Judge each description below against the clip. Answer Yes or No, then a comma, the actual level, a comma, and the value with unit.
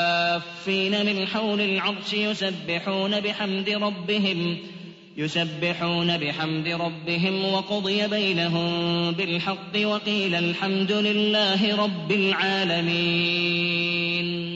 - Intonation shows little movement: No, average, 3.0 semitones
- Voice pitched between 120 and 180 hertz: No, high, 190 Hz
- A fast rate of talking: No, average, 70 wpm